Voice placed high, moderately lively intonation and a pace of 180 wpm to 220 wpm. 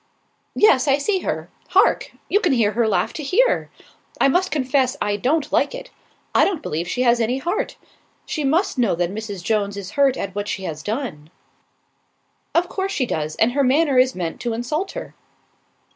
No: very high, 255 Hz; wide, 6.9 semitones; average, 190 wpm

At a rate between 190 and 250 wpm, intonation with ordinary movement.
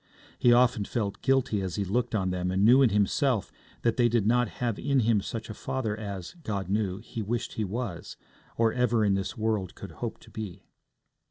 Yes: fast, 205 wpm; average, 3.3 semitones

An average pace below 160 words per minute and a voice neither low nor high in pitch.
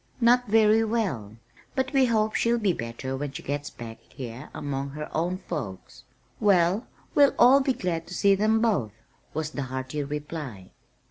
No: average, 170 wpm; medium, 165 Hz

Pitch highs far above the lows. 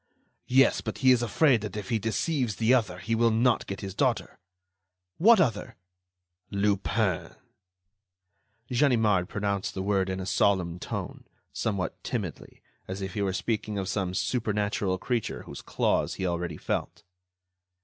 No: average, 3.6 semitones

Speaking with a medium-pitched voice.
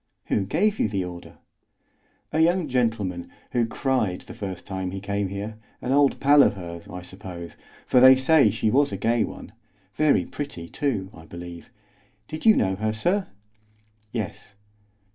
No: low, 110 Hz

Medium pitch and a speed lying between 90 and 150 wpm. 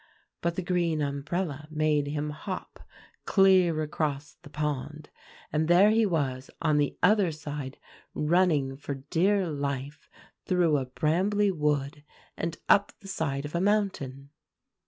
Yes: medium, 155 Hz; slow, 135 wpm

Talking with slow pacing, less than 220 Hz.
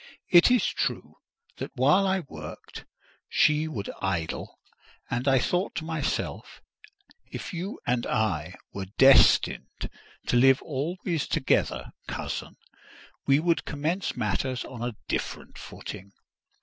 Yes: slow, 125 wpm; low, 135 Hz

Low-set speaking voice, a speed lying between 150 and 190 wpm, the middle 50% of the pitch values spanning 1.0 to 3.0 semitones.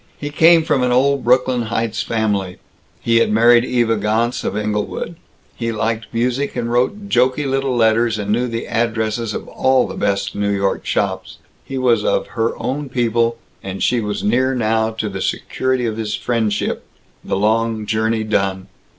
Yes: low, 115 Hz; average, 175 wpm; narrow, 2.6 semitones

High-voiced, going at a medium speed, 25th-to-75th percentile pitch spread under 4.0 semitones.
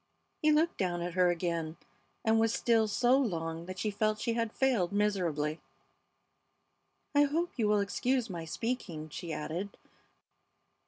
No: high, 205 Hz; average, 150 wpm; average, 5.3 semitones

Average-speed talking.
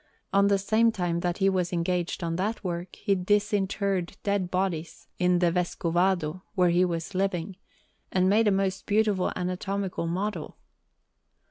Yes: average, 150 wpm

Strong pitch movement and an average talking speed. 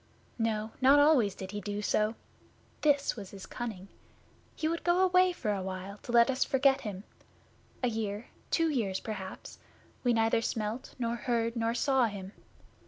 No: average, 4.4 semitones; average, 170 wpm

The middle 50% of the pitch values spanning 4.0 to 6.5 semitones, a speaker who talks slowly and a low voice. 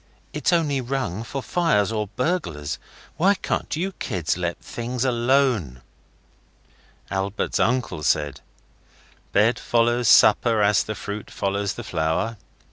Yes: average, 5.0 semitones; slow, 125 wpm; low, 110 Hz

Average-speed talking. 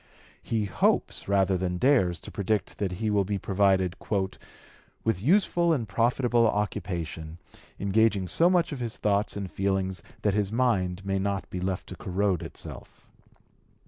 Yes: average, 150 wpm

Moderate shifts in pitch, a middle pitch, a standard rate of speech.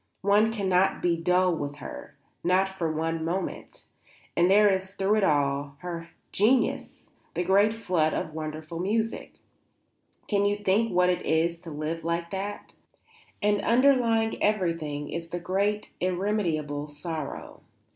Yes: average, 3.9 semitones; medium, 180 Hz; average, 145 wpm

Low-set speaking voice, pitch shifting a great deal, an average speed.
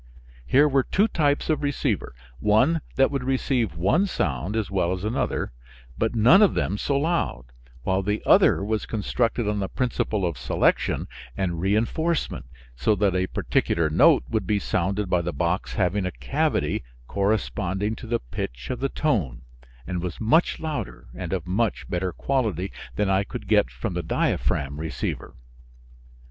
Yes: low, 100 Hz; wide, 6.0 semitones; average, 165 wpm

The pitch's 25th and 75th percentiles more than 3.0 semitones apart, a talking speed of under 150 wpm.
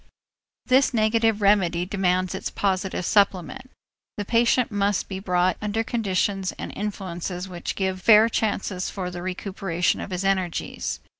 No: narrow, 2.5 semitones; average, 140 wpm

